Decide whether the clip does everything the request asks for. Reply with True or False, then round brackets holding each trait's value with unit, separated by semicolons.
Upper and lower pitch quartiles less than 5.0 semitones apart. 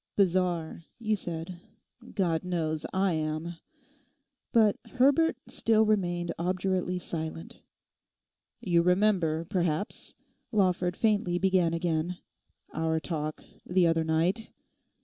True (2.8 semitones)